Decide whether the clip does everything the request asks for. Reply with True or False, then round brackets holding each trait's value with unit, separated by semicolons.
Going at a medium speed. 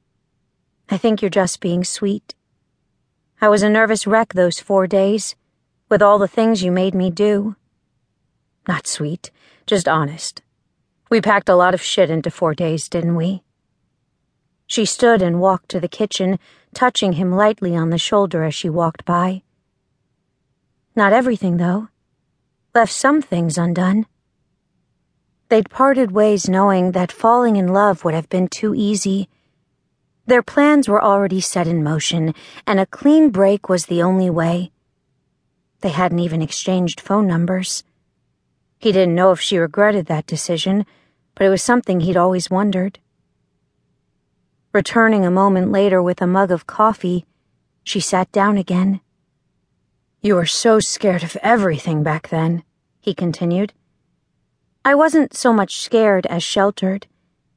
True (145 wpm)